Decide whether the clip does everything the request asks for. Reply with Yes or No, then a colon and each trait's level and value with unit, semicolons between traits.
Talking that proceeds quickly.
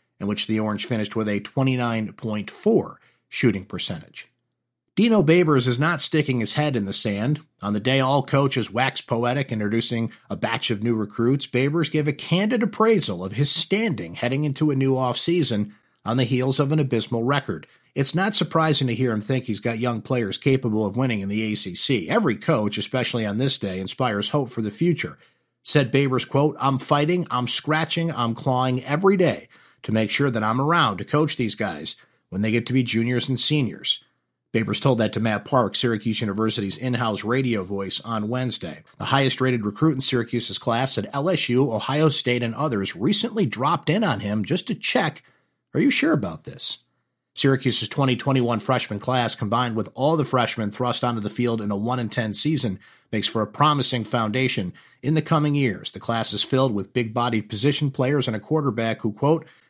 No: average, 190 wpm